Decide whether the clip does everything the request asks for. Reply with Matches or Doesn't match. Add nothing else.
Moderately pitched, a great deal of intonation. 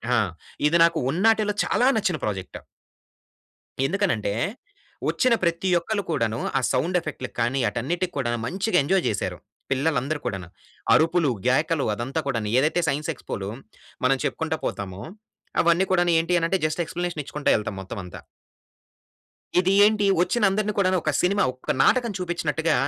Matches